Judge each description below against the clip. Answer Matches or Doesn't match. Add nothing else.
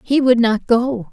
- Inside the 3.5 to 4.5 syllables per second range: Matches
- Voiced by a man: Doesn't match